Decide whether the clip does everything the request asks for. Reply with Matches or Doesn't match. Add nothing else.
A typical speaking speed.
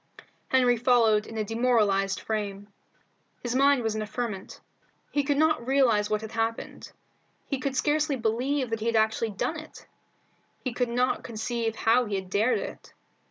Matches